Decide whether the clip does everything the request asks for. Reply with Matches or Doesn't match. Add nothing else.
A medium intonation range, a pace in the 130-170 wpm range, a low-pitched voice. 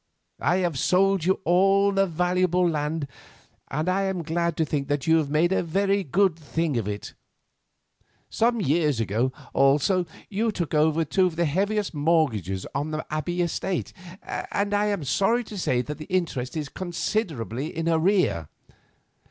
Doesn't match